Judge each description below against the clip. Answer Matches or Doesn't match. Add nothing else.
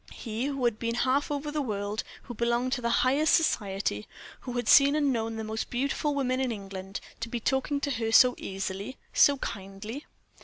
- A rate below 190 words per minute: Doesn't match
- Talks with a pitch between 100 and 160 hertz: Doesn't match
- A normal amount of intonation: Matches